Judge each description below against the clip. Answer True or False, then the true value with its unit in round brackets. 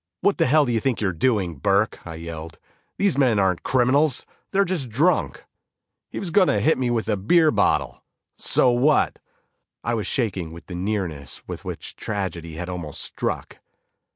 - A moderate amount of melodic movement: False (7.1 semitones)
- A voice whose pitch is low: True (110 Hz)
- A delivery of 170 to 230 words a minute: True (180 wpm)